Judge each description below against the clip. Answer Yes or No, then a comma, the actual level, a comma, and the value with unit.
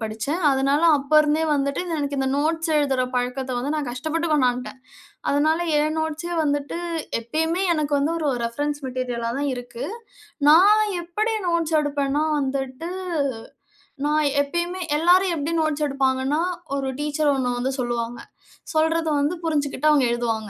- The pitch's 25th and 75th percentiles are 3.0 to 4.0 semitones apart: Yes, average, 3.3 semitones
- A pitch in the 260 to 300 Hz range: Yes, very high, 290 Hz